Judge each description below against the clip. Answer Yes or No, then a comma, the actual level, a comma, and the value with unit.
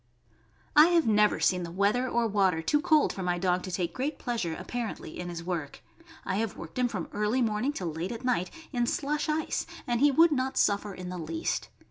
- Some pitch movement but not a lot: No, wide, 6.2 semitones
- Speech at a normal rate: No, fast, 215 wpm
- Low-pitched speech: No, high, 210 Hz